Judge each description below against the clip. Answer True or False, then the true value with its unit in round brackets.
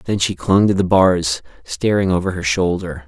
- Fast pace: False (195 wpm)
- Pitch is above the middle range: False (90 Hz)